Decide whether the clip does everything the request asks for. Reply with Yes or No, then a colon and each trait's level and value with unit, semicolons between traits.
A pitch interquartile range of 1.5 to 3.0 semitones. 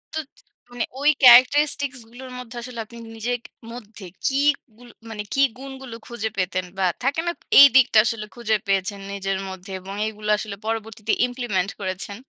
No: average, 3.8 semitones